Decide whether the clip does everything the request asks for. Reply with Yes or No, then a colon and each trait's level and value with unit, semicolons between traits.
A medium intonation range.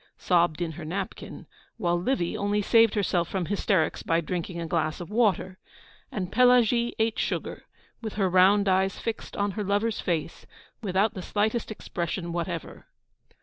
Yes: average, 3.6 semitones